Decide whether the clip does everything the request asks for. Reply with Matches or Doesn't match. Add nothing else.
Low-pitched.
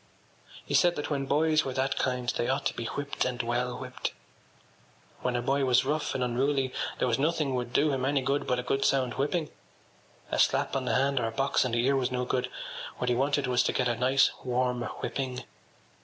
Matches